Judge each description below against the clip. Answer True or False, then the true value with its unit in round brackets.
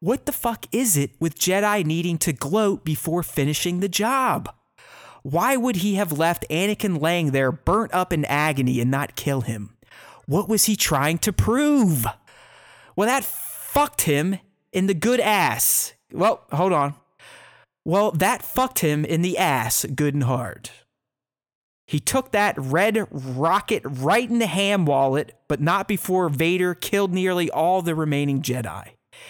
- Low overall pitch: False (175 Hz)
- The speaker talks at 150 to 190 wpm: True (160 wpm)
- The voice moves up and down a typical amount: False (6.1 semitones)